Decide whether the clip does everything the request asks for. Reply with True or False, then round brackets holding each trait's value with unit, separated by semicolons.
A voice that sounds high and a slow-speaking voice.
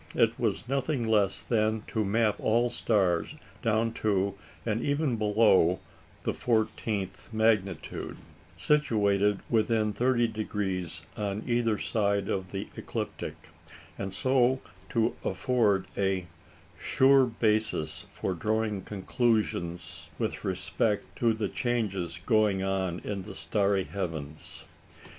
False (105 Hz; 110 wpm)